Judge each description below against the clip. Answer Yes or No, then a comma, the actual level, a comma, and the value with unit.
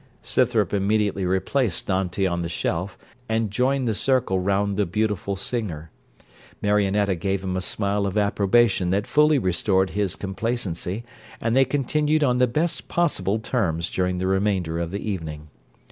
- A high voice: No, low, 100 Hz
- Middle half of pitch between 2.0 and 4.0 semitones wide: Yes, average, 3.5 semitones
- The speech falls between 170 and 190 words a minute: No, average, 155 wpm